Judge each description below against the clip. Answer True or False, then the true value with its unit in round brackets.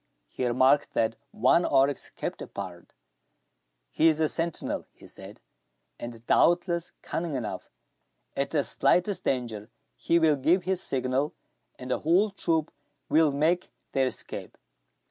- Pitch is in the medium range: True (145 Hz)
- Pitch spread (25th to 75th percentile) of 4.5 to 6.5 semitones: True (4.8 semitones)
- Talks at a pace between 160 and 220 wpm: False (135 wpm)